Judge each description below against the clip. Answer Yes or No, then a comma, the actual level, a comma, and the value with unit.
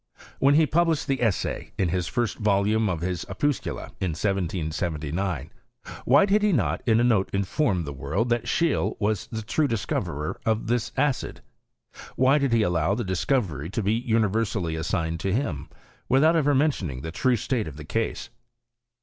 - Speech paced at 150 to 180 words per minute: Yes, average, 160 wpm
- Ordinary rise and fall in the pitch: No, wide, 6.5 semitones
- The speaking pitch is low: Yes, low, 105 Hz